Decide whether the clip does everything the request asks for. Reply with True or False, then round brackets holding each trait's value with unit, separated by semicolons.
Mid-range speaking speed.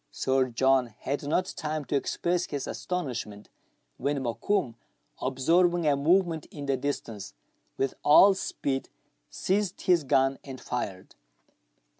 False (125 wpm)